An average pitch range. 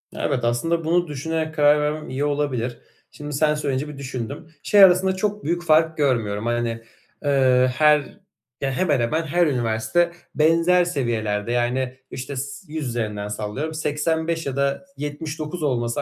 Yes: average, 4.3 semitones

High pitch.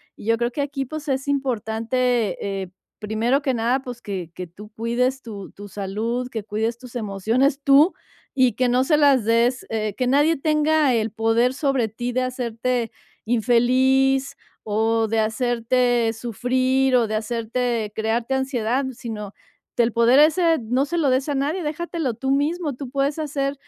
Yes: high, 245 Hz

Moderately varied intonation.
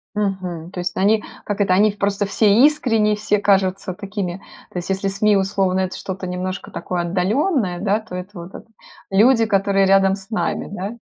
No: narrow, 2.1 semitones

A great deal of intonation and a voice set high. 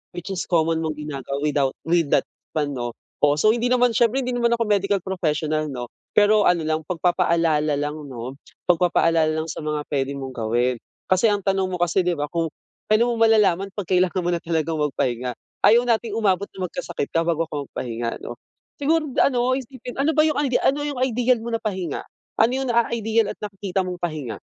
No: wide, 6.6 semitones; medium, 180 Hz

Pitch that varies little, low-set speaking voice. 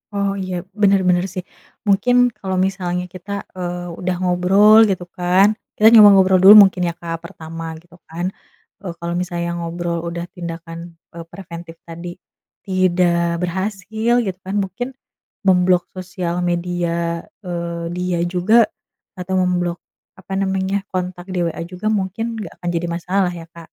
No: narrow, 1.8 semitones; medium, 180 Hz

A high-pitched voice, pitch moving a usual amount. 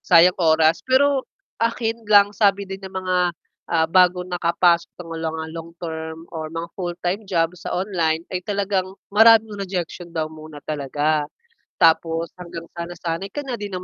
No: medium, 175 Hz; average, 3.2 semitones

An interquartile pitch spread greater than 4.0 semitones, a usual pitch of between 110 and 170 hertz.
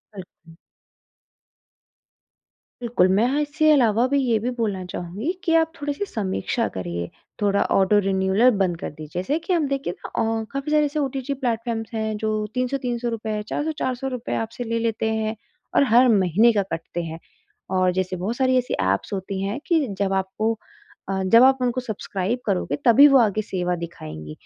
No: average, 5.2 semitones; high, 225 Hz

